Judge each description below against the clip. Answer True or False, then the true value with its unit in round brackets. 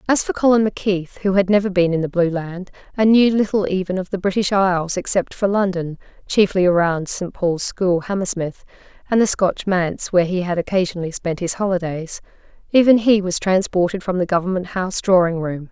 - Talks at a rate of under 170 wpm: False (180 wpm)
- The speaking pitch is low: False (185 Hz)